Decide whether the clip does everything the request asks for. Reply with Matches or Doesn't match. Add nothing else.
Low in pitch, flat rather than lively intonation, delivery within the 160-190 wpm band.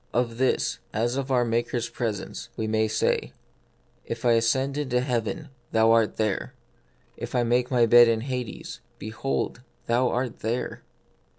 Matches